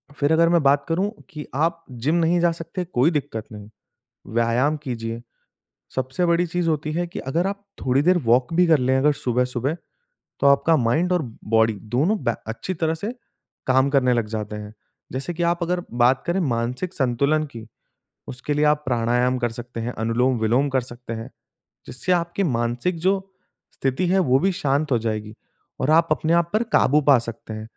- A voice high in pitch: No, medium, 140 Hz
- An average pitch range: No, wide, 5.8 semitones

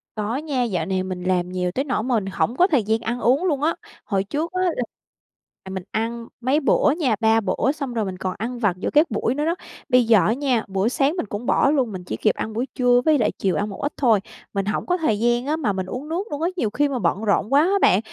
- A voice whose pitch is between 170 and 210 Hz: No, high, 235 Hz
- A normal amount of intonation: No, wide, 5.7 semitones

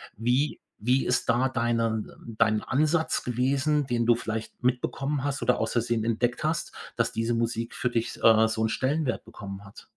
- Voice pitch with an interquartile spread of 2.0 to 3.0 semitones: Yes, narrow, 2.6 semitones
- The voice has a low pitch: Yes, low, 120 Hz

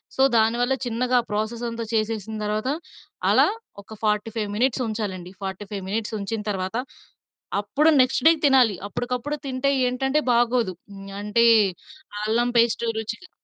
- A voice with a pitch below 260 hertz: Yes, high, 230 Hz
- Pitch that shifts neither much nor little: Yes, average, 3.1 semitones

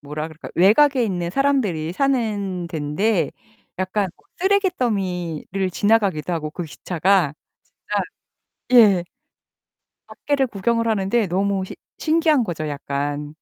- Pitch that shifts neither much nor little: No, wide, 5.8 semitones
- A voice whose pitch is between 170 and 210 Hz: Yes, high, 190 Hz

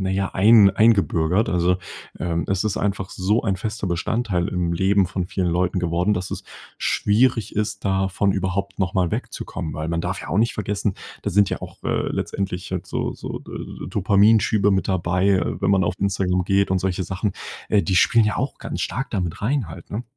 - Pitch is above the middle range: No, very low, 95 Hz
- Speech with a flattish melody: Yes, narrow, 2.3 semitones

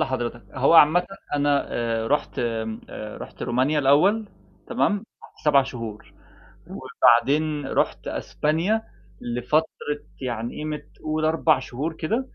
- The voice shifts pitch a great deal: No, average, 4.5 semitones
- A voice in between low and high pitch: Yes, medium, 145 Hz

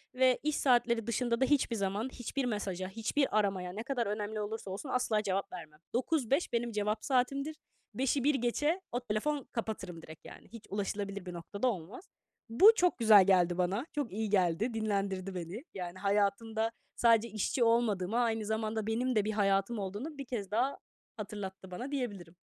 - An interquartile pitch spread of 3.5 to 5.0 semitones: Yes, average, 3.8 semitones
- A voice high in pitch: Yes, high, 220 Hz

